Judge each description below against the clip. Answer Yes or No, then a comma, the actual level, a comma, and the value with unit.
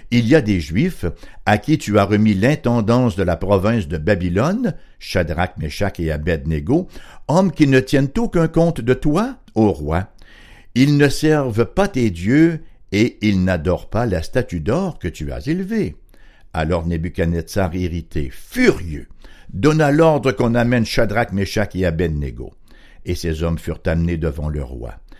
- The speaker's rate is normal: Yes, average, 160 wpm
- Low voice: Yes, low, 105 Hz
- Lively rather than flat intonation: Yes, wide, 8.0 semitones